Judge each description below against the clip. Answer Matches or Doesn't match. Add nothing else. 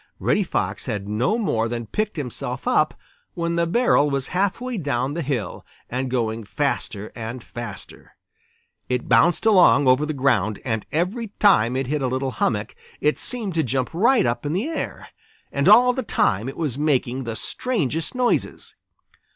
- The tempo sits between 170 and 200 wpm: Matches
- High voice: Doesn't match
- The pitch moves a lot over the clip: Matches